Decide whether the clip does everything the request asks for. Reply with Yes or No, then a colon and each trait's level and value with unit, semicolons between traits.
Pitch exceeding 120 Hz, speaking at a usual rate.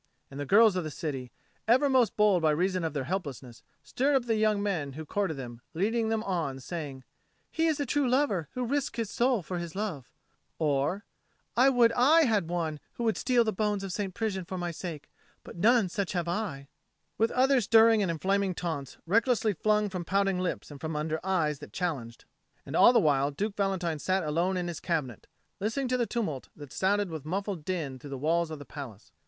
No: medium, 185 Hz; fast, 215 wpm